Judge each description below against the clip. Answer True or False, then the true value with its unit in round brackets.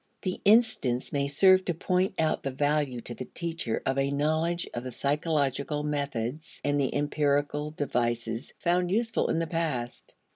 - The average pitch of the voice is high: False (145 Hz)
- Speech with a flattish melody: False (3.7 semitones)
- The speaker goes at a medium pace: True (160 wpm)